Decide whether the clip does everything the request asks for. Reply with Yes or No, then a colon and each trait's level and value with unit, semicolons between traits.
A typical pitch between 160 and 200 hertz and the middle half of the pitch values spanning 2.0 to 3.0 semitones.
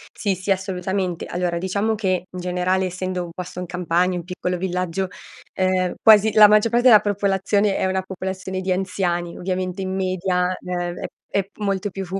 No: medium, 185 Hz; narrow, 1.3 semitones